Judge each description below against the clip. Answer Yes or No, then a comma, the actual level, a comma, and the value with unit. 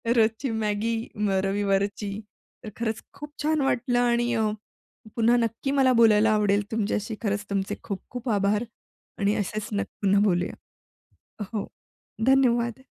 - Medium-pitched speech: No, high, 220 Hz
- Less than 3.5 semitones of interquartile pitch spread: Yes, average, 2.8 semitones